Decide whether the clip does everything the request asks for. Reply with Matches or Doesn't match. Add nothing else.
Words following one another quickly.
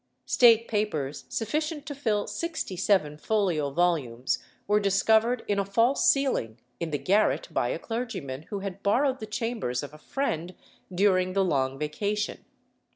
Doesn't match